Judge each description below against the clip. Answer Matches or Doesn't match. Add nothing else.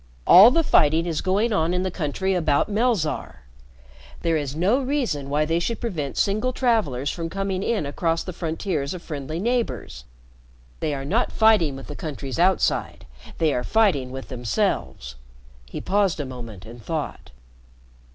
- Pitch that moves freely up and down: Matches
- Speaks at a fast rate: Doesn't match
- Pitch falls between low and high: Matches